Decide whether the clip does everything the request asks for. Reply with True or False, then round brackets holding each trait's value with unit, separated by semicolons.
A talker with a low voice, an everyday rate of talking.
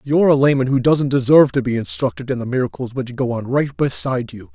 False (130 Hz; 235 wpm)